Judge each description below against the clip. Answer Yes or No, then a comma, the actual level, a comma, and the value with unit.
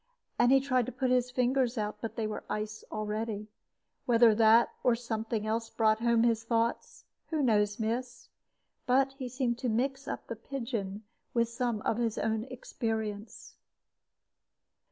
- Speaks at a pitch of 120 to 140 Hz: No, high, 230 Hz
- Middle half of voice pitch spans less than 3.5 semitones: Yes, narrow, 2.4 semitones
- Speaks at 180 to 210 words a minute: No, average, 155 wpm